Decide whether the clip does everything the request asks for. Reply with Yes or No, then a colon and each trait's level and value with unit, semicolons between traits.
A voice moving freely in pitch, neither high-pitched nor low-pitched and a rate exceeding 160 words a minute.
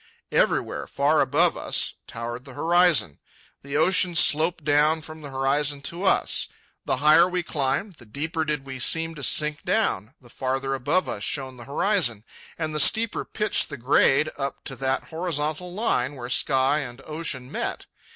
No: average, 3.6 semitones; medium, 145 Hz; average, 170 wpm